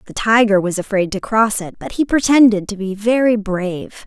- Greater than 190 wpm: Yes, fast, 205 wpm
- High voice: Yes, high, 210 Hz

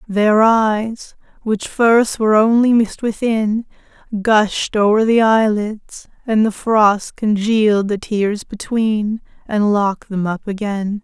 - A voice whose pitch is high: Yes, high, 215 Hz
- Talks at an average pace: No, slow, 130 wpm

